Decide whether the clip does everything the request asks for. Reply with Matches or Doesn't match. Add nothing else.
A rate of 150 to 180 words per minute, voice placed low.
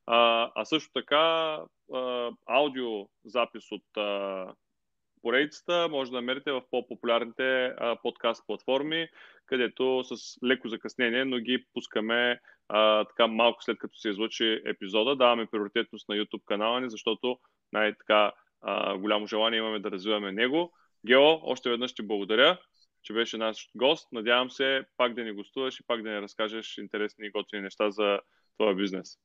Doesn't match